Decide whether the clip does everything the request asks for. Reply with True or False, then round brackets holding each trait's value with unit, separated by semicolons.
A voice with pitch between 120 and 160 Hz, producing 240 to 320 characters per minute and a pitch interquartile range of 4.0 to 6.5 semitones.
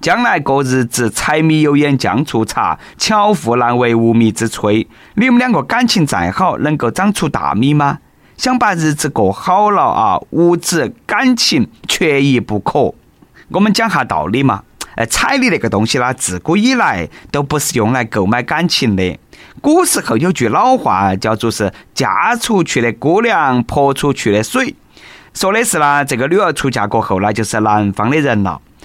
False (135 Hz; 250 characters per minute; 7.4 semitones)